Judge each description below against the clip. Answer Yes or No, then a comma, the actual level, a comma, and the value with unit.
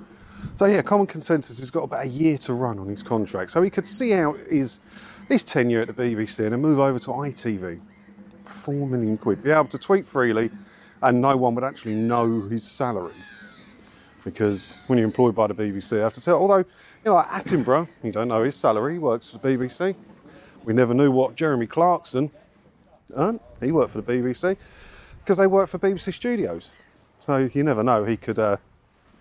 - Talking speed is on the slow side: No, average, 200 wpm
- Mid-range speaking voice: No, low, 125 Hz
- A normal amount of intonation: No, wide, 6.2 semitones